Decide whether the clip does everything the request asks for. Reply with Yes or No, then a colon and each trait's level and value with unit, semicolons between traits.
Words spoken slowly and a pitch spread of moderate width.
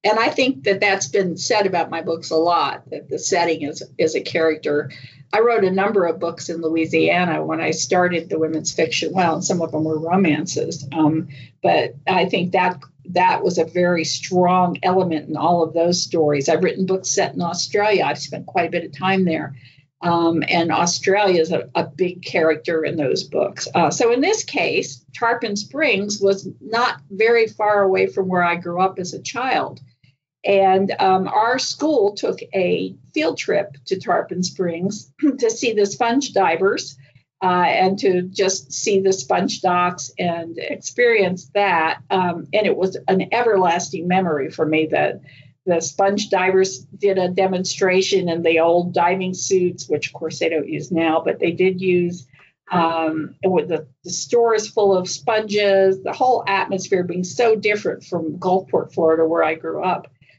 No: average, 180 wpm; average, 3.3 semitones